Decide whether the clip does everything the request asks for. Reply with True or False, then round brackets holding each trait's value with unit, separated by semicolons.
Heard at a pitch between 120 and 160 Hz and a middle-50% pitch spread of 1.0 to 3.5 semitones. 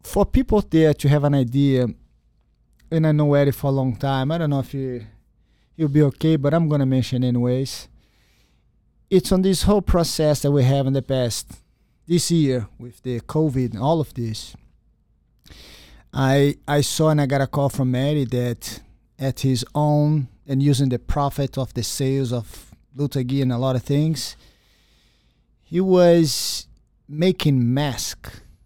True (140 Hz; 3.2 semitones)